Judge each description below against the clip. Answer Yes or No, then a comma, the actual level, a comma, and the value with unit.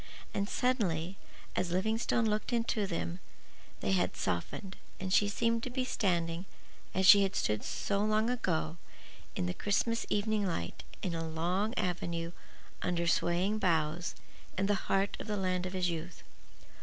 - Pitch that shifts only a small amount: No, average, 3.7 semitones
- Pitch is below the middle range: No, high, 190 Hz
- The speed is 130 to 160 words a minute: Yes, average, 155 wpm